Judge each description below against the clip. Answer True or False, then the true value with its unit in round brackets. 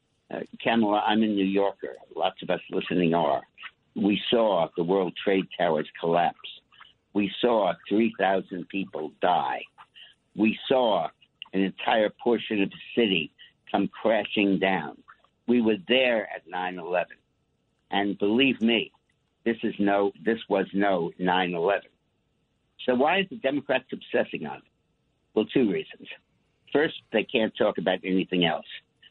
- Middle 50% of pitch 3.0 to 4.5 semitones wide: False (2.6 semitones)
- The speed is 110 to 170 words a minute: True (140 wpm)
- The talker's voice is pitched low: True (100 Hz)